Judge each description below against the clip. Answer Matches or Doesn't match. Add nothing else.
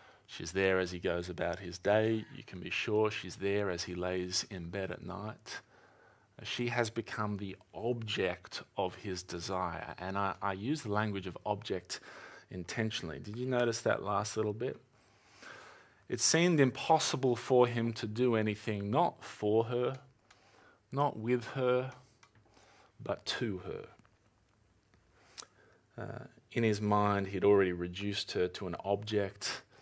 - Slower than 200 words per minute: Matches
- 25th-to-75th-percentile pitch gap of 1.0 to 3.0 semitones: Doesn't match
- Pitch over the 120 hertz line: Doesn't match